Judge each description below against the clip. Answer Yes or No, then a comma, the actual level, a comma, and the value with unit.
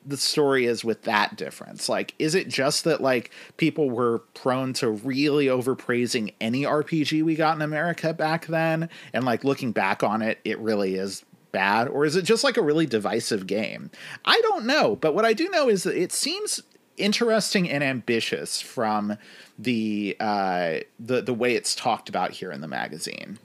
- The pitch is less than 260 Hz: Yes, medium, 140 Hz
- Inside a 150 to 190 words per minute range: Yes, average, 185 wpm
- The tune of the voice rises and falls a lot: Yes, wide, 5.9 semitones